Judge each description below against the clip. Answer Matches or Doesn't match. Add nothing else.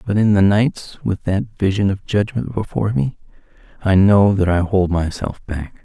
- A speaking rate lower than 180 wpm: Doesn't match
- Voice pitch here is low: Matches